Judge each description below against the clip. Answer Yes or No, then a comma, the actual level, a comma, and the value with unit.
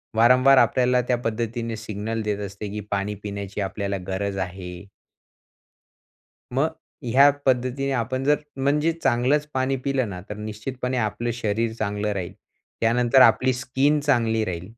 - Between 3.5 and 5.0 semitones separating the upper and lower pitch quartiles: Yes, average, 4.0 semitones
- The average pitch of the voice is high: No, low, 115 Hz